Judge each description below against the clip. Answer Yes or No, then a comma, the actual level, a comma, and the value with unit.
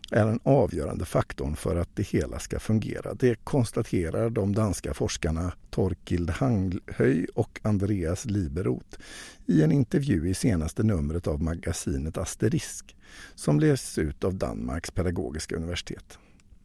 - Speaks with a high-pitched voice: No, very low, 95 Hz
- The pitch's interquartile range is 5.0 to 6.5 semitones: Yes, wide, 5.4 semitones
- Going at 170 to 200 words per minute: No, average, 130 wpm